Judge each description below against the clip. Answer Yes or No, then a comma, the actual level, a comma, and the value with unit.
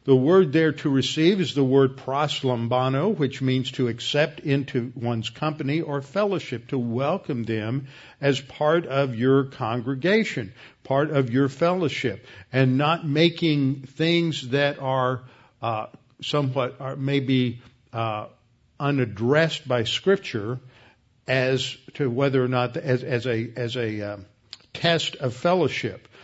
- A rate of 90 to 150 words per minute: Yes, slow, 135 wpm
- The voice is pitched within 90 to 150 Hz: Yes, low, 135 Hz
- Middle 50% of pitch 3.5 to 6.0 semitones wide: No, average, 3.0 semitones